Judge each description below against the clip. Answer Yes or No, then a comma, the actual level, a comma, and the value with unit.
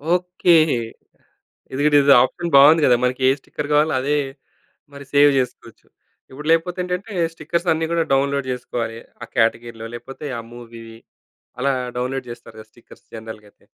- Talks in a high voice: No, medium, 140 Hz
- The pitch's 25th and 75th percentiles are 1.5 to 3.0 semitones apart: No, average, 4.6 semitones